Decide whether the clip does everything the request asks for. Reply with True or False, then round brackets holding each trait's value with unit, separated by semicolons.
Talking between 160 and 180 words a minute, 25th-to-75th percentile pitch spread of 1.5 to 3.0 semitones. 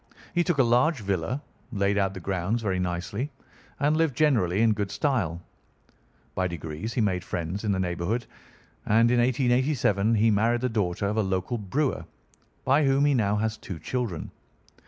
False (175 wpm; 5.0 semitones)